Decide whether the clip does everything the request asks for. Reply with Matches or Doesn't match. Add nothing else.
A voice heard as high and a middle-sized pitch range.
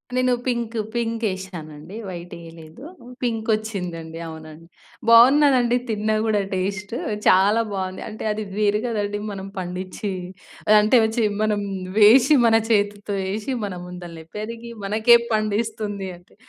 Matches